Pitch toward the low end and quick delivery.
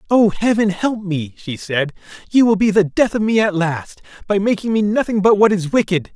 No: high, 200 Hz; fast, 225 wpm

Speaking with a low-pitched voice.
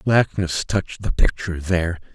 Yes: very low, 90 Hz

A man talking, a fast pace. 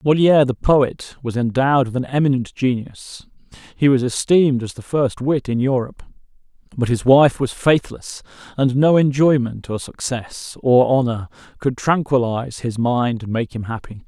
No: male; average, 160 wpm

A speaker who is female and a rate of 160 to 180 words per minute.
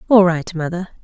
Yes: female; average, 175 wpm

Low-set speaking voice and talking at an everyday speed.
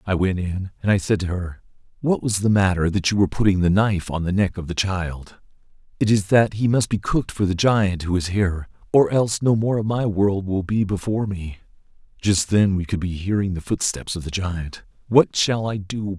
No: low, 100 Hz; fast, 235 wpm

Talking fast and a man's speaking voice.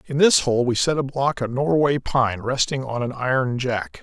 Yes: fast, 225 wpm; male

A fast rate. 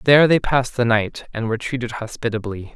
No: average, 195 wpm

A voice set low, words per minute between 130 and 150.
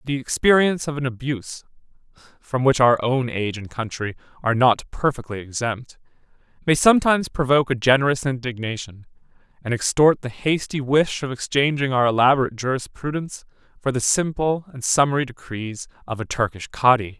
Yes: low, 130 Hz; average, 145 wpm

